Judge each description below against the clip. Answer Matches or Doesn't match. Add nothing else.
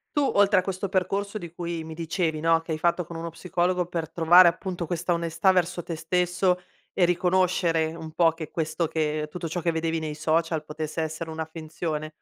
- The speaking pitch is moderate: Matches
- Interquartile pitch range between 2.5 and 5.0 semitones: Doesn't match